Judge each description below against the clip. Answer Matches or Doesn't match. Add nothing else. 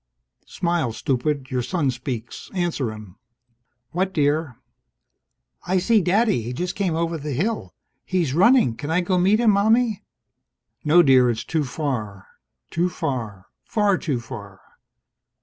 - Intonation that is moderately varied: Doesn't match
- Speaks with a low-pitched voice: Doesn't match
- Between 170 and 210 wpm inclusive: Doesn't match